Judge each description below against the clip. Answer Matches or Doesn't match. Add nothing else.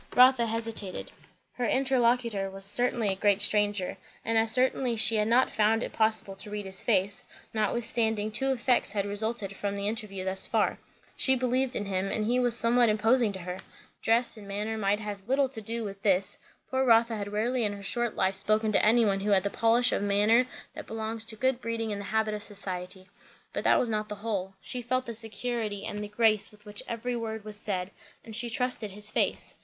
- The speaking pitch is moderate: Doesn't match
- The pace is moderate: Doesn't match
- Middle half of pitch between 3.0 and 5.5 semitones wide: Doesn't match